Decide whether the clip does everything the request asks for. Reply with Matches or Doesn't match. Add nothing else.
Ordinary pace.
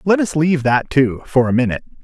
Doesn't match